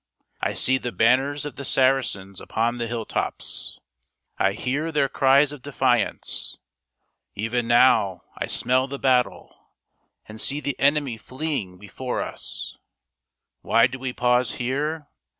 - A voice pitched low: Yes, low, 130 Hz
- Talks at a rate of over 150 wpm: No, slow, 135 wpm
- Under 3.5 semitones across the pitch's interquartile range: Yes, average, 3.0 semitones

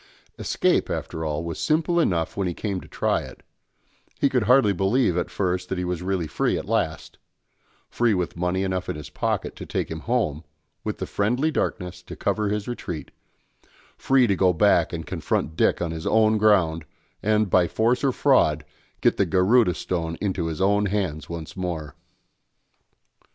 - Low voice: Yes, very low, 95 Hz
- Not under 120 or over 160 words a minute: No, average, 180 wpm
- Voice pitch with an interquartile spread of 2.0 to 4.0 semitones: No, average, 4.4 semitones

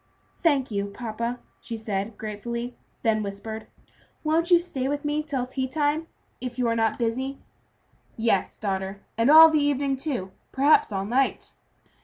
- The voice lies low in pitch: No, high, 245 Hz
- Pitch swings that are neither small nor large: Yes, average, 4.8 semitones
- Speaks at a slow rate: No, average, 155 wpm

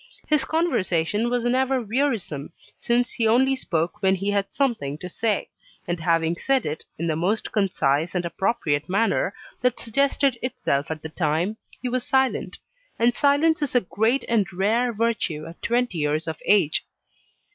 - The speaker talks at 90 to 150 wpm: No, average, 165 wpm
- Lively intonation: Yes, wide, 6.8 semitones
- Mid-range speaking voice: No, high, 210 Hz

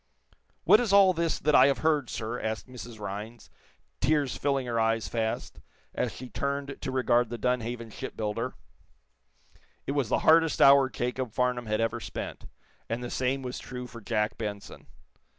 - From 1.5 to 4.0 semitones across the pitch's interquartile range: Yes, average, 3.4 semitones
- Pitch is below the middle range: Yes, low, 125 Hz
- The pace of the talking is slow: No, average, 170 wpm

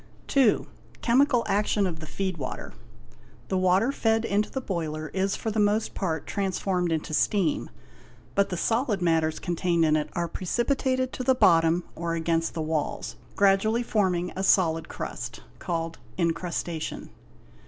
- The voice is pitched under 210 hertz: Yes, medium, 185 Hz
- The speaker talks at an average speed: Yes, average, 155 wpm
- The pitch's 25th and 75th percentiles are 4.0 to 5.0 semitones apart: Yes, average, 4.4 semitones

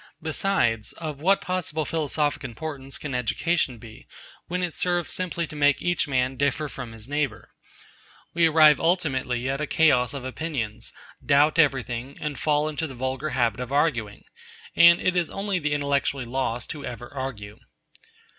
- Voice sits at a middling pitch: Yes, medium, 145 Hz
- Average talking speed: Yes, average, 160 wpm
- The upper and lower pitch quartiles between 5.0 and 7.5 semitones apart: No, average, 4.0 semitones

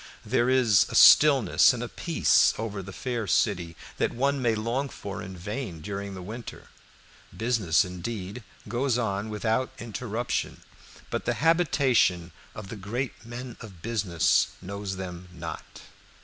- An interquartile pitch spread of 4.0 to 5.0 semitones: Yes, average, 4.3 semitones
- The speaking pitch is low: Yes, low, 110 Hz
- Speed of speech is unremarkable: Yes, average, 145 wpm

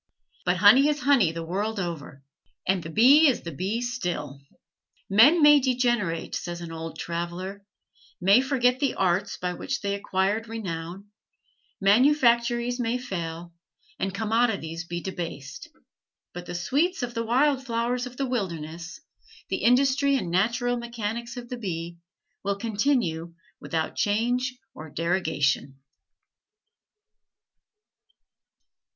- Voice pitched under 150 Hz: No, high, 205 Hz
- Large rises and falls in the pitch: Yes, wide, 6.1 semitones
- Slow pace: Yes, slow, 125 wpm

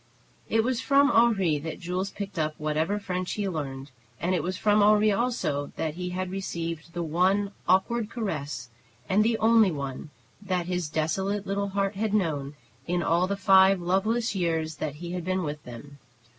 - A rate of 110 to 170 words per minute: No, average, 180 wpm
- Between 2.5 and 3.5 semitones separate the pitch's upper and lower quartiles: No, average, 4.2 semitones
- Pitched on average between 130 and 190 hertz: Yes, medium, 185 Hz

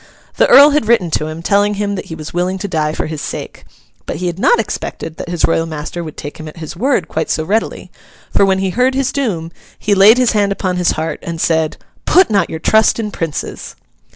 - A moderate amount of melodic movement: Yes, average, 4.7 semitones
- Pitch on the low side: No, medium, 180 Hz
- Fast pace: Yes, fast, 235 wpm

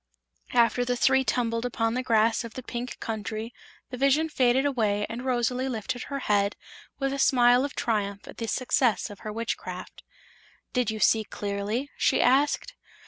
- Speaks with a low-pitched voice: No, high, 240 Hz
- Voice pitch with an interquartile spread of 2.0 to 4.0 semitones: Yes, average, 2.9 semitones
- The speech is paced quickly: No, average, 170 wpm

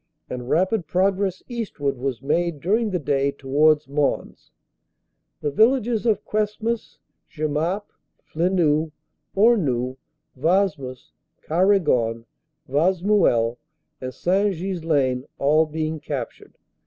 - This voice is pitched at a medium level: Yes, medium, 160 Hz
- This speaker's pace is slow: Yes, slow, 95 wpm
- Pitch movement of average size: No, wide, 5.9 semitones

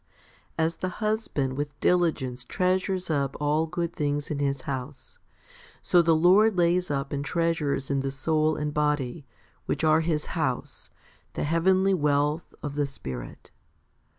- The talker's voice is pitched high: No, medium, 150 Hz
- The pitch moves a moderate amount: Yes, average, 3.4 semitones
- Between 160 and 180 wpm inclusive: No, average, 150 wpm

